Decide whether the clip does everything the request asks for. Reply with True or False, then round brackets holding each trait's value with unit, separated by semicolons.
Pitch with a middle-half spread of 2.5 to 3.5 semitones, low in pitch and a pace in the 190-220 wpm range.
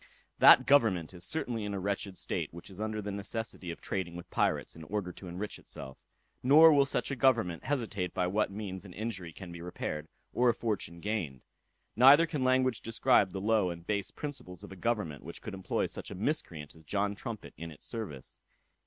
False (4.6 semitones; 100 Hz; 205 wpm)